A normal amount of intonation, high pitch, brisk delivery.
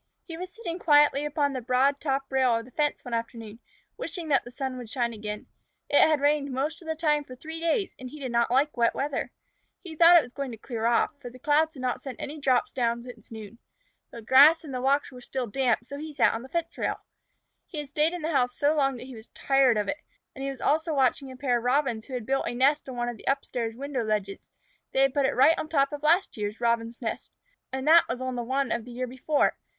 Yes: average, 3.5 semitones; very high, 270 Hz; fast, 260 wpm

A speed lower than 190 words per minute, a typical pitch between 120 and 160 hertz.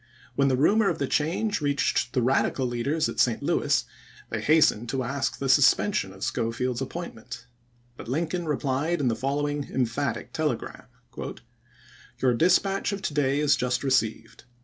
Yes: average, 160 wpm; medium, 140 Hz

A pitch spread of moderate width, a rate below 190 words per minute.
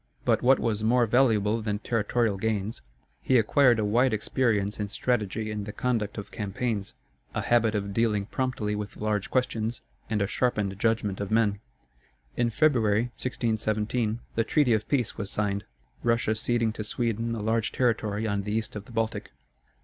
No: narrow, 2.3 semitones; average, 170 wpm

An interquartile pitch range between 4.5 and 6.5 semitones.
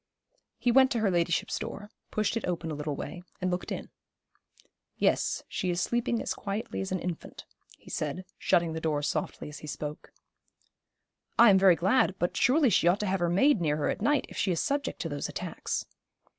Yes: average, 5.0 semitones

